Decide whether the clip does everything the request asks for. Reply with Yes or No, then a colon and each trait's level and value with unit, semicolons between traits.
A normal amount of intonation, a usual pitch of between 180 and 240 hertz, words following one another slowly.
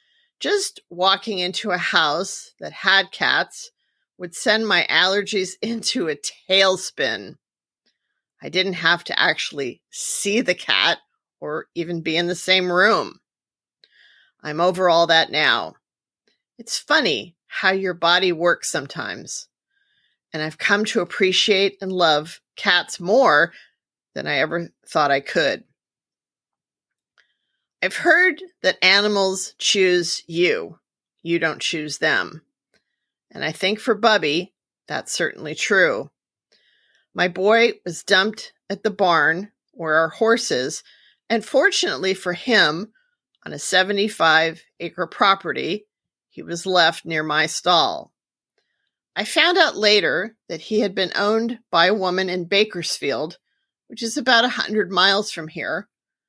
Yes: average, 4.2 semitones; high, 190 Hz; slow, 130 wpm